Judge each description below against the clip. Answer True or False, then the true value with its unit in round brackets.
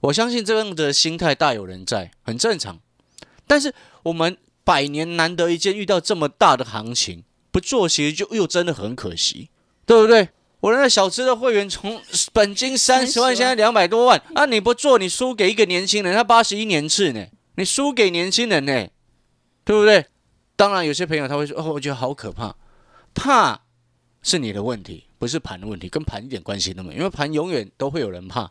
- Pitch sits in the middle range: True (175 Hz)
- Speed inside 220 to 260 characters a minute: False (300 characters per minute)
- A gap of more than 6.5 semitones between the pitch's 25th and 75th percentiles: True (9.0 semitones)